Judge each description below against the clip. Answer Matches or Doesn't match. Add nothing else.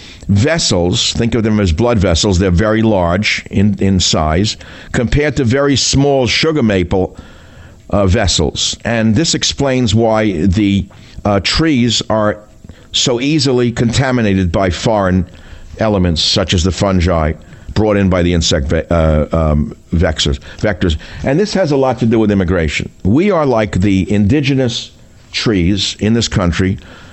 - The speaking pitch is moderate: Doesn't match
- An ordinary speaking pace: Matches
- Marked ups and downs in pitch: Doesn't match